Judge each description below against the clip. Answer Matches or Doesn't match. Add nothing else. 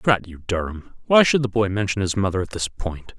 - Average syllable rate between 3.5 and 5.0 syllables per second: Doesn't match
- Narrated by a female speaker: Doesn't match